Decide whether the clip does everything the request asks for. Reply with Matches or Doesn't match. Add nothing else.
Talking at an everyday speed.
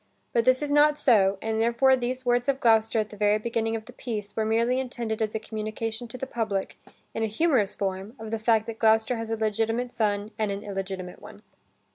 Doesn't match